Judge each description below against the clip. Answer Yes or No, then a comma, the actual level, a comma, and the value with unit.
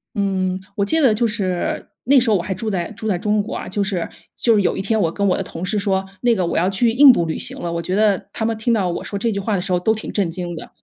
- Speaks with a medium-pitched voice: No, high, 200 Hz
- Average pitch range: Yes, average, 3.1 semitones